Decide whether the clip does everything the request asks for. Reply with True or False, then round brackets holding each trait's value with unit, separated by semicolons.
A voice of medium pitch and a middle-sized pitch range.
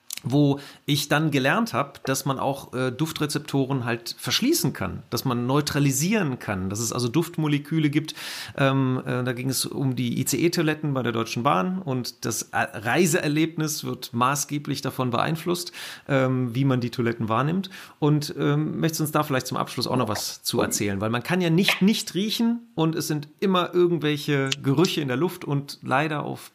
True (145 Hz; 4.0 semitones)